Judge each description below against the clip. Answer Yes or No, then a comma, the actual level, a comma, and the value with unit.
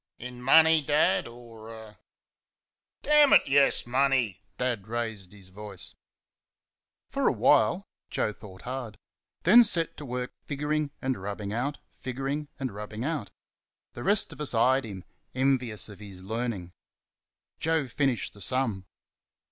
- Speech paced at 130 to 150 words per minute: Yes, average, 140 wpm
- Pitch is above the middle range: No, low, 120 Hz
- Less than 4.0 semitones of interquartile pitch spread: No, average, 4.8 semitones